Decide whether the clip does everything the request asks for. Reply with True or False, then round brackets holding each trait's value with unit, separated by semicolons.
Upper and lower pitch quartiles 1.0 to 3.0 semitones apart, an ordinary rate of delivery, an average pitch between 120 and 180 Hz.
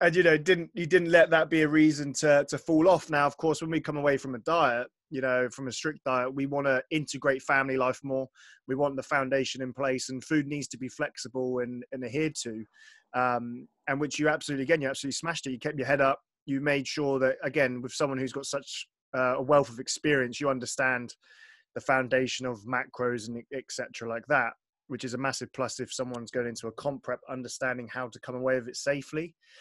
False (2.7 semitones; 230 wpm; 135 Hz)